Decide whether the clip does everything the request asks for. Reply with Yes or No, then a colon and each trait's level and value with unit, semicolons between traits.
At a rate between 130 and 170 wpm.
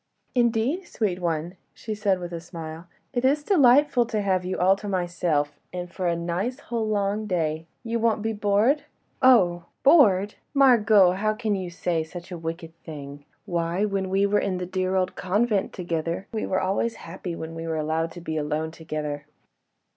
No: average, 185 wpm